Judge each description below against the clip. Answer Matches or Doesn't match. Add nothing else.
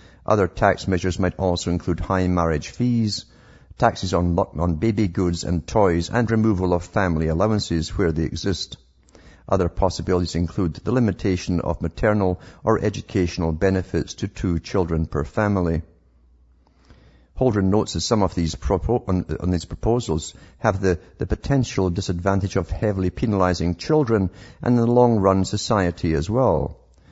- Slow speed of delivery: Doesn't match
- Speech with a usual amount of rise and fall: Matches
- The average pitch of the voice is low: Matches